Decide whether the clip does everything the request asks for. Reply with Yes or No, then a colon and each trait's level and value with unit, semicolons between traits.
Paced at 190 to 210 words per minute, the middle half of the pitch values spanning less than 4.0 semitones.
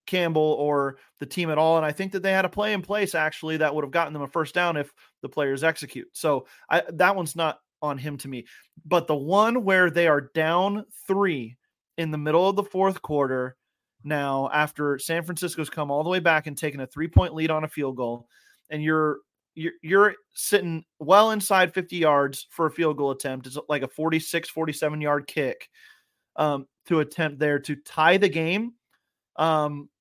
Yes: average, 200 wpm; average, 3.3 semitones